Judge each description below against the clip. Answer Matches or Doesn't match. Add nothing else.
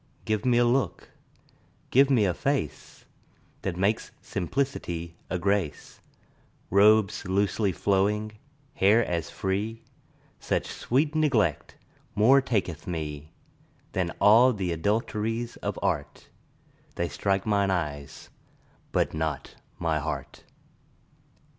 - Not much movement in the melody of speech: Doesn't match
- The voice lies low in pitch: Matches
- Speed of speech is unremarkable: Doesn't match